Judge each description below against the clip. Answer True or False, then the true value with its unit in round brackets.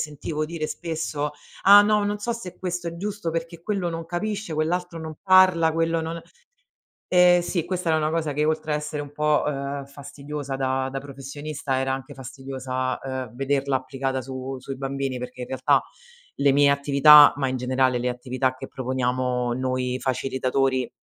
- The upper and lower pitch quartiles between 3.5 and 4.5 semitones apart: True (3.9 semitones)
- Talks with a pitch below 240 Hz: True (140 Hz)